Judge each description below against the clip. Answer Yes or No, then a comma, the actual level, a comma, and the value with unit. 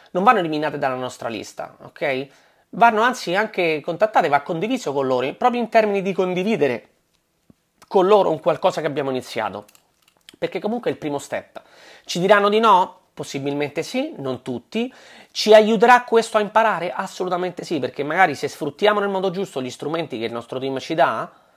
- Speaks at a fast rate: Yes, fast, 175 wpm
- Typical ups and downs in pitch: No, wide, 7.2 semitones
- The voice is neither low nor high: Yes, medium, 180 Hz